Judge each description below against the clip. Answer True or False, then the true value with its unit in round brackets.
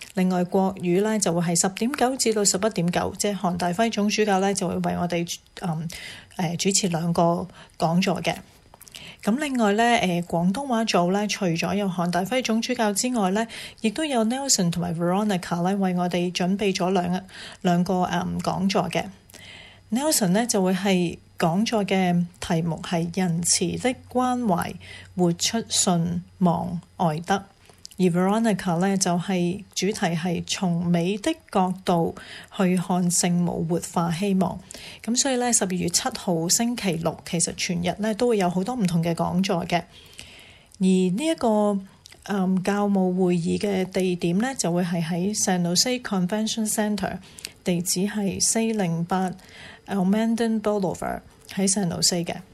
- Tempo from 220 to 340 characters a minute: True (285 characters per minute)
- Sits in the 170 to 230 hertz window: True (185 Hz)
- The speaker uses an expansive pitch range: False (3.1 semitones)